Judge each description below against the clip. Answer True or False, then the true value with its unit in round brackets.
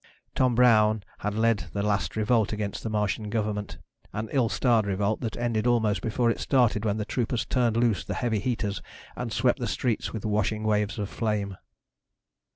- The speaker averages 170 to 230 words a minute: True (180 wpm)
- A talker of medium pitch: False (110 Hz)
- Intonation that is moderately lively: False (1.9 semitones)